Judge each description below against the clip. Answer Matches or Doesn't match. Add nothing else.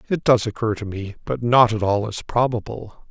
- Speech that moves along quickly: Matches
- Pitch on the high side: Doesn't match